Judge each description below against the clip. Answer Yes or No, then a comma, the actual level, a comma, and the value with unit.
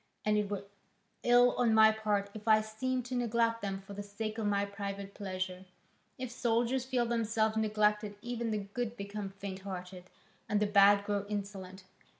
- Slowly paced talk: No, average, 175 wpm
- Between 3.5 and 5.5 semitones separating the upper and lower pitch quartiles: No, narrow, 2.4 semitones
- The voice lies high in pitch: Yes, high, 210 Hz